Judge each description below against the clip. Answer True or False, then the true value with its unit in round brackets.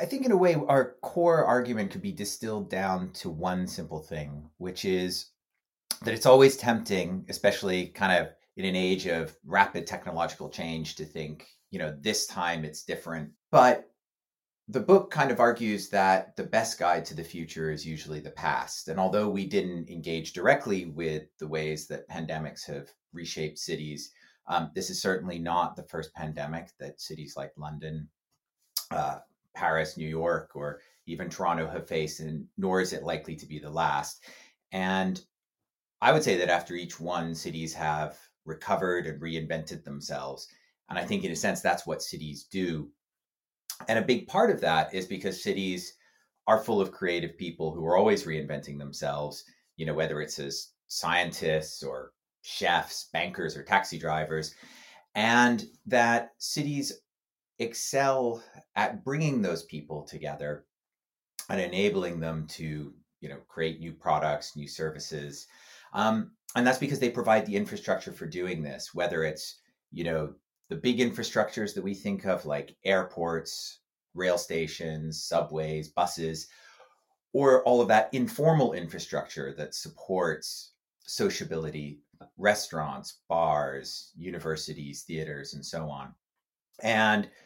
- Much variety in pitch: False (4.2 semitones)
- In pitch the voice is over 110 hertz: False (85 Hz)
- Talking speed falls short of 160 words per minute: True (150 wpm)